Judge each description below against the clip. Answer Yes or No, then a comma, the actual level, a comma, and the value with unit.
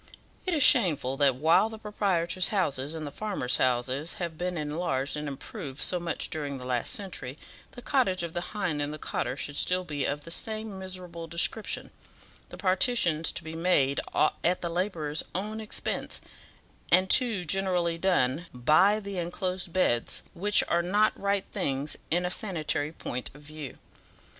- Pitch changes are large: No, average, 4.5 semitones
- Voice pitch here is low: No, medium, 170 Hz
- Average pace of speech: Yes, average, 165 wpm